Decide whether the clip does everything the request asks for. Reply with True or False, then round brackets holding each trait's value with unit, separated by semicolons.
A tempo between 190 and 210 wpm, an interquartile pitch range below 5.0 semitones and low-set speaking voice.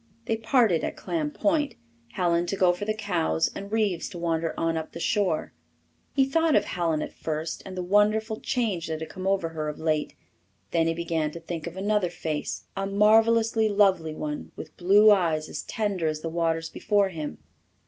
False (195 wpm; 4.4 semitones; 180 Hz)